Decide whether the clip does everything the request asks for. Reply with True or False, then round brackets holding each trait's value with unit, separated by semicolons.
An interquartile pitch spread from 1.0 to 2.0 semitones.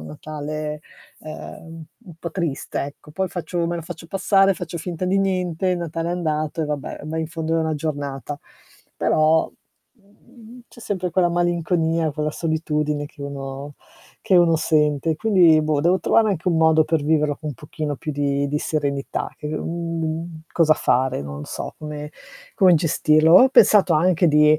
False (2.5 semitones)